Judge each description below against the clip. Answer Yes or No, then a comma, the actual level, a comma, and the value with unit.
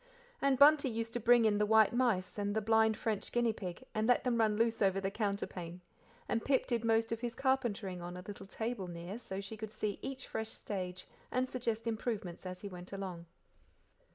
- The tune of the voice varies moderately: Yes, average, 3.4 semitones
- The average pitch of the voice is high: Yes, high, 220 Hz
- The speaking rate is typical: No, fast, 210 wpm